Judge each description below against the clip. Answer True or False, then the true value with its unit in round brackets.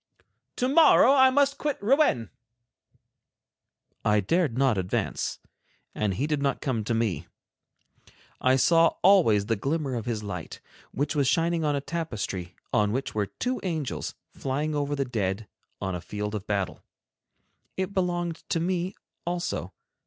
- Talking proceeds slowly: False (150 wpm)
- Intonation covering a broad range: True (8.4 semitones)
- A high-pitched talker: False (140 Hz)